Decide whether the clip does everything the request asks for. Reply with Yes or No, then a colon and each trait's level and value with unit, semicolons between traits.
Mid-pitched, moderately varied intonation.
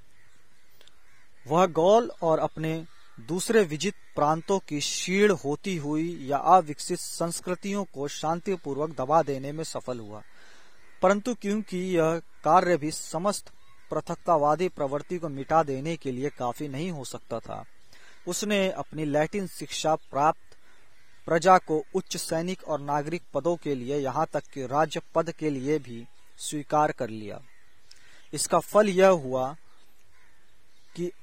Yes: medium, 160 Hz; average, 3.8 semitones